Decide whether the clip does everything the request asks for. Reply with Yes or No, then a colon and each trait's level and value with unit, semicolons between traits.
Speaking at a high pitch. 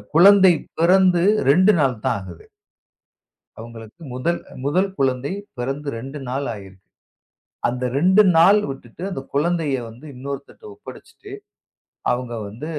No: medium, 140 Hz